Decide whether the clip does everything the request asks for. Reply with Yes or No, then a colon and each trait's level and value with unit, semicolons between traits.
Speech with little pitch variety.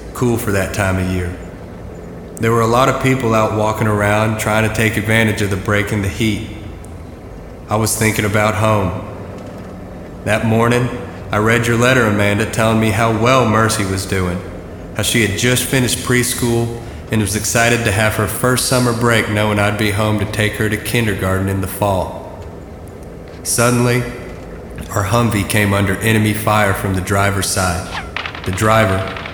No: average, 3.0 semitones